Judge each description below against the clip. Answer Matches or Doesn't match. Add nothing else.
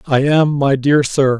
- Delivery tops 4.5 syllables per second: Doesn't match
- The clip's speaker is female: Doesn't match